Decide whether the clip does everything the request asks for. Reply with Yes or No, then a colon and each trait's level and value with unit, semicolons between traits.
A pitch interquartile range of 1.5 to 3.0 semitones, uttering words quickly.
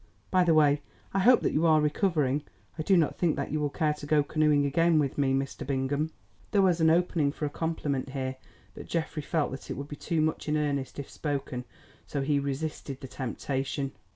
Yes: narrow, 2.5 semitones; fast, 215 wpm